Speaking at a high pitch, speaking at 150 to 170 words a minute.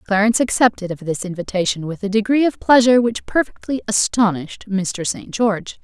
Yes: high, 210 Hz; average, 165 wpm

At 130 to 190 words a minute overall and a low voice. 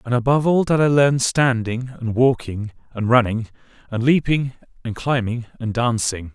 Yes: average, 160 wpm; low, 120 Hz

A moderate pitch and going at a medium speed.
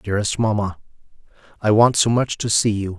No: low, 105 Hz; average, 160 wpm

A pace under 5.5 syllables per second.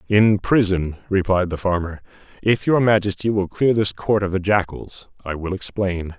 Yes: 4.8 syllables/s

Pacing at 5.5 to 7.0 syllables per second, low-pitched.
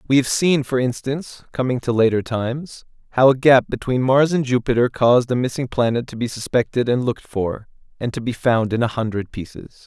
No: 5.1 syllables/s; low, 125 Hz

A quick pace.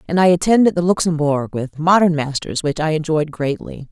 No: average, 185 wpm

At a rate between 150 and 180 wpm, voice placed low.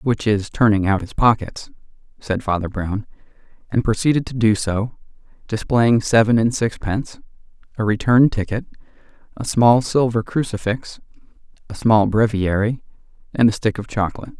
No: average, 140 wpm; low, 110 Hz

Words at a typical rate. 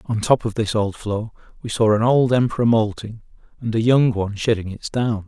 No: fast, 215 wpm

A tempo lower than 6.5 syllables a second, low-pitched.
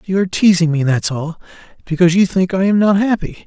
No: 5.3 syllables/s; medium, 180 Hz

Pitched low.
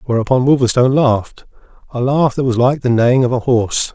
Yes: low, 125 Hz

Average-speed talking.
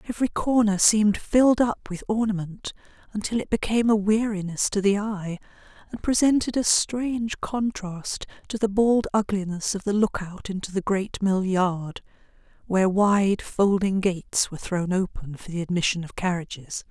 Yes: average, 160 wpm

